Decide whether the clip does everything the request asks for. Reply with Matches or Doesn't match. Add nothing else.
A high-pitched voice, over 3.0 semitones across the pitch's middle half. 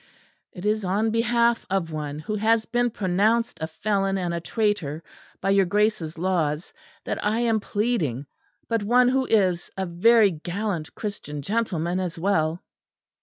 Matches